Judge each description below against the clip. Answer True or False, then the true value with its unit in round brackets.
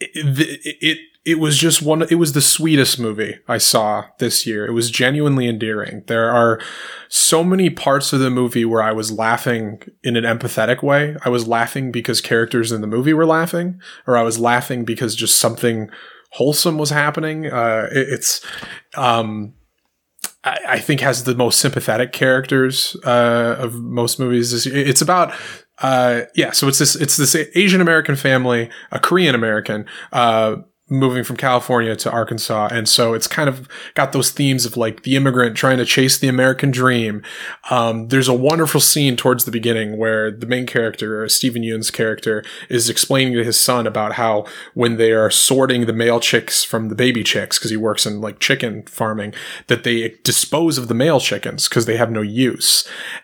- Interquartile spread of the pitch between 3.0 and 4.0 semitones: True (3.5 semitones)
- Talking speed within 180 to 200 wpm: True (185 wpm)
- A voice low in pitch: True (120 Hz)